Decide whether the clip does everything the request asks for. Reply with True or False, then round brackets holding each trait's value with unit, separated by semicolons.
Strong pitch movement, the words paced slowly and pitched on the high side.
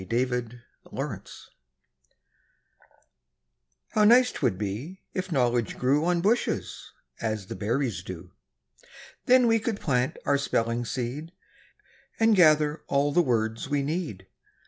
False (7.0 semitones; 120 wpm; 140 Hz)